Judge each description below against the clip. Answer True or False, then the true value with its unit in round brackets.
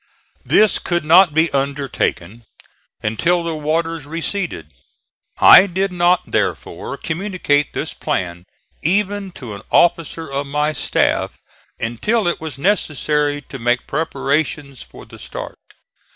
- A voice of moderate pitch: True (155 Hz)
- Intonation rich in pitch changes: False (4.1 semitones)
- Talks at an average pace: False (125 wpm)